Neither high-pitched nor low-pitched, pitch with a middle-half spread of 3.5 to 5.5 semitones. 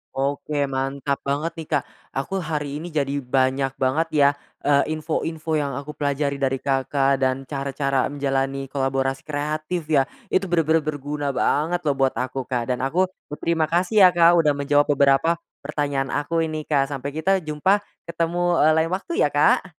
No: medium, 145 Hz; average, 2.7 semitones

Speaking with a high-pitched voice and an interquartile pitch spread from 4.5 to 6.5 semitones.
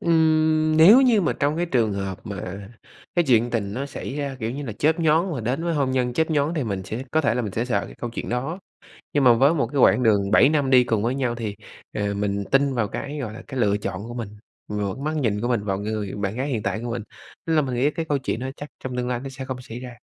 No: low, 125 Hz; average, 5.1 semitones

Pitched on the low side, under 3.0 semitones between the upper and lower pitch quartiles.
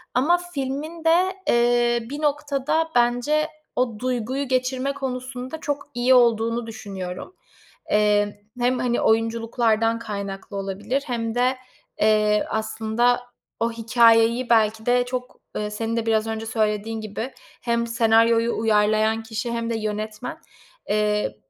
No: high, 230 Hz; narrow, 2.6 semitones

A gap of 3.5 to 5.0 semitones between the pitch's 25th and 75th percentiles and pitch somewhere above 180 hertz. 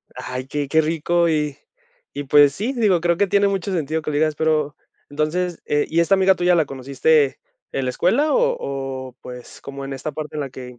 No: average, 4.1 semitones; medium, 155 Hz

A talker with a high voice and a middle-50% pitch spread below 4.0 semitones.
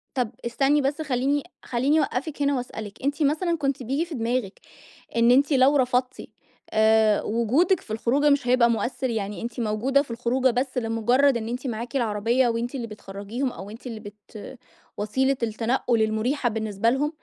Yes: high, 245 Hz; average, 3.5 semitones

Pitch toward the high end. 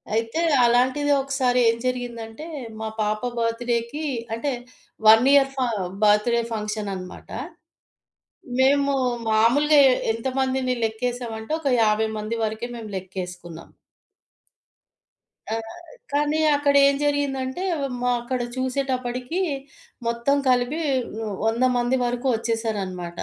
Yes: high, 240 Hz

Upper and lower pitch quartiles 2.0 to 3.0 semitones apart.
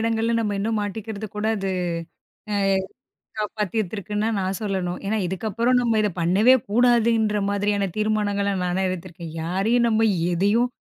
Yes: narrow, 2.5 semitones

